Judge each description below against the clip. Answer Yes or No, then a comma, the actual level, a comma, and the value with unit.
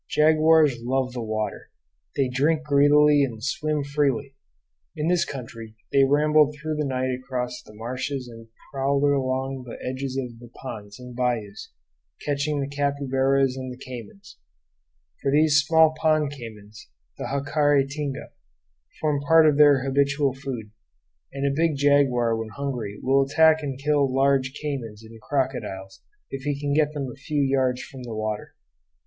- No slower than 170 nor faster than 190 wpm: No, average, 155 wpm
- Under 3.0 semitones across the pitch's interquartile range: Yes, narrow, 2.5 semitones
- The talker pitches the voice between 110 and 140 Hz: Yes, low, 135 Hz